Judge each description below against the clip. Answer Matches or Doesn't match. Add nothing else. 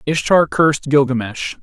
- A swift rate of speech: Doesn't match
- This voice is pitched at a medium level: Matches